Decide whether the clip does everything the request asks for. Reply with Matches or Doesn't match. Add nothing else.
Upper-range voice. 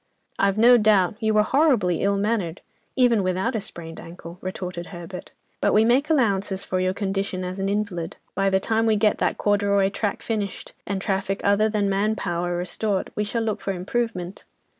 Matches